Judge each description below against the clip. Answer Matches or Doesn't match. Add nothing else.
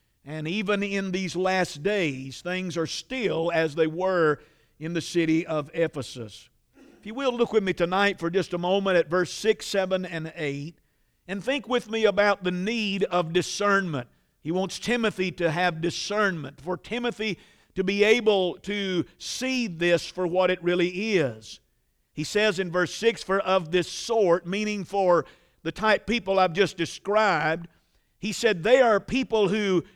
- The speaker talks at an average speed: Matches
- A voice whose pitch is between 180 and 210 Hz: Matches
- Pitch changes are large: Doesn't match